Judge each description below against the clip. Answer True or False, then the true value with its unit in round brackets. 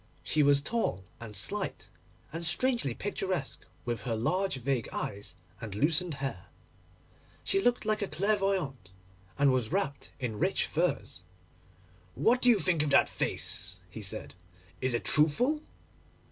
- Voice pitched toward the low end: False (145 Hz)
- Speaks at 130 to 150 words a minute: True (145 wpm)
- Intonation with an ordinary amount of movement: False (8.7 semitones)